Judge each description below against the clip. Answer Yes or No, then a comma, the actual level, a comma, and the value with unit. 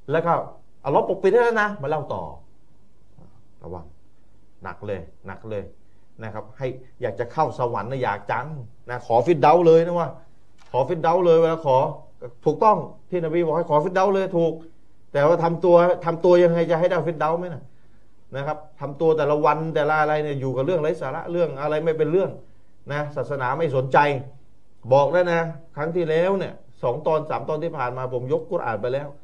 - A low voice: No, medium, 150 Hz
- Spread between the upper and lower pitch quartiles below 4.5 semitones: No, average, 5.1 semitones